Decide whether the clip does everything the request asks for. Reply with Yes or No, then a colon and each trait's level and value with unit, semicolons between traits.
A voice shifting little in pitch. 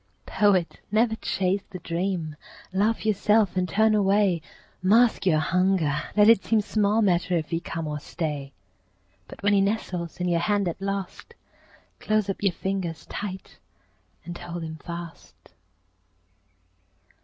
No: average, 3.3 semitones